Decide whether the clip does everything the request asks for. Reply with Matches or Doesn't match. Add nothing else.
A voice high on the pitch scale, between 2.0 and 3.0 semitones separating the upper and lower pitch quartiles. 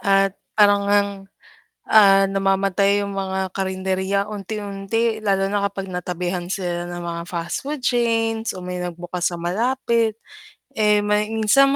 Matches